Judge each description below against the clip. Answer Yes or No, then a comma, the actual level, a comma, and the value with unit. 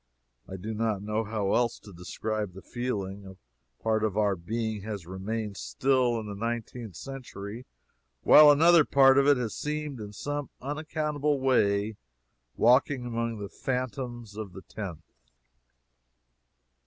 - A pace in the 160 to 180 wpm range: No, average, 140 wpm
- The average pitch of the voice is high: No, low, 115 Hz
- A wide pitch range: No, average, 4.5 semitones